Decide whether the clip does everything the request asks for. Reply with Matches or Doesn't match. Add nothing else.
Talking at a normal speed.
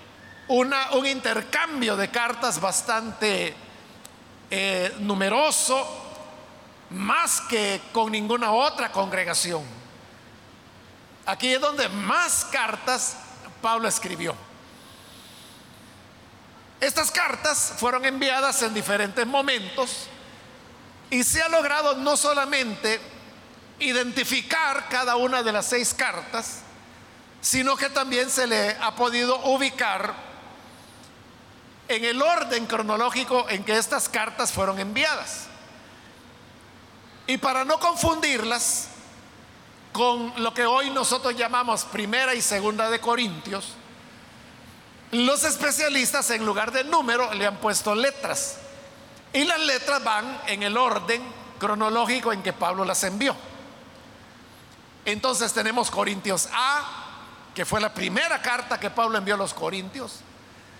Doesn't match